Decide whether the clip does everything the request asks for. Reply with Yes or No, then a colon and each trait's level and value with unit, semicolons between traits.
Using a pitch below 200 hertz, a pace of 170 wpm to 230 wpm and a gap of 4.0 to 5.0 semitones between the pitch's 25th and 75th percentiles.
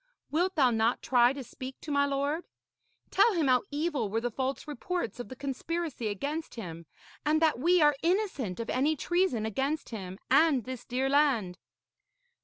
No: very high, 275 Hz; average, 175 wpm; average, 4.6 semitones